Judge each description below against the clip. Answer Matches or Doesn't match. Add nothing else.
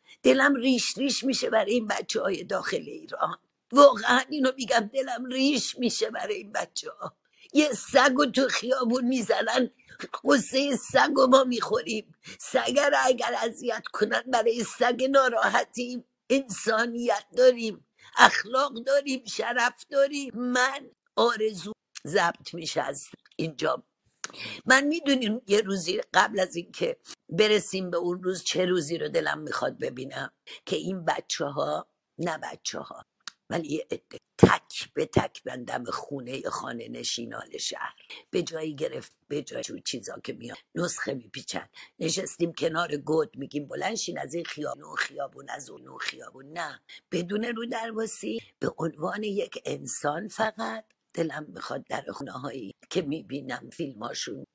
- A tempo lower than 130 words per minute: Doesn't match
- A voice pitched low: Doesn't match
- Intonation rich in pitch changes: Matches